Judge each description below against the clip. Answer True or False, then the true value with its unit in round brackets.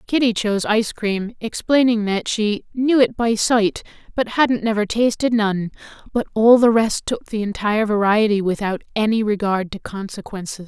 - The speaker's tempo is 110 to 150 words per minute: False (165 wpm)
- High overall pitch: True (215 Hz)